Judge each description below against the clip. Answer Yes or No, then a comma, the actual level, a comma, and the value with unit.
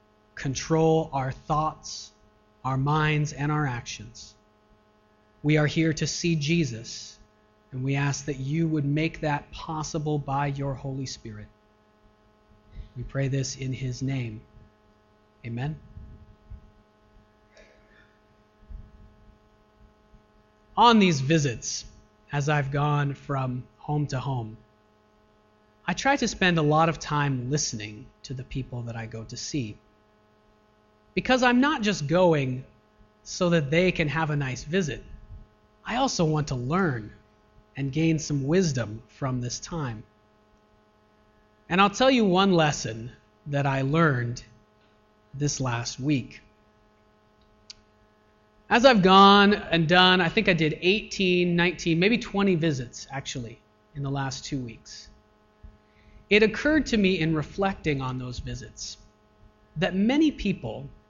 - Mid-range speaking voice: No, low, 130 Hz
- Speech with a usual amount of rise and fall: No, wide, 6.6 semitones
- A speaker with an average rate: No, slow, 130 wpm